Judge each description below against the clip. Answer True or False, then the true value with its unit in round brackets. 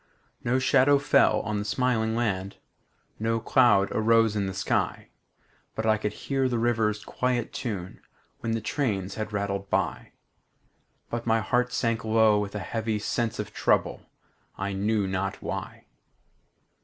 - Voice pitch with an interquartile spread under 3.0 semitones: True (2.5 semitones)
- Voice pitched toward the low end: True (110 Hz)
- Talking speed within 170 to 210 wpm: False (145 wpm)